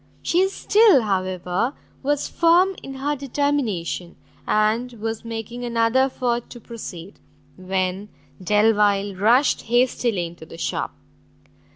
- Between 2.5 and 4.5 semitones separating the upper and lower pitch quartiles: No, average, 5.2 semitones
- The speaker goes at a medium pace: No, slow, 110 wpm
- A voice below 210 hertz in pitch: No, high, 230 Hz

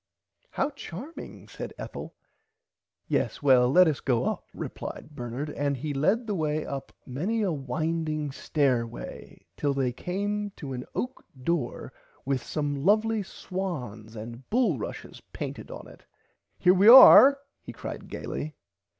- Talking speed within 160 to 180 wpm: No, average, 140 wpm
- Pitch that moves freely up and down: Yes, wide, 6.7 semitones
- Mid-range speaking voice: Yes, medium, 150 Hz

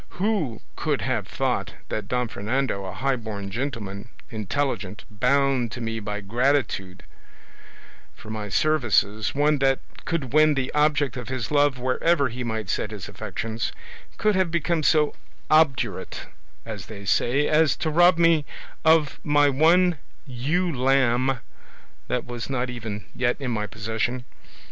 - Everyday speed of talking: Yes, average, 145 wpm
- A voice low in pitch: Yes, low, 130 Hz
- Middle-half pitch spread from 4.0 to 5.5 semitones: Yes, average, 5.0 semitones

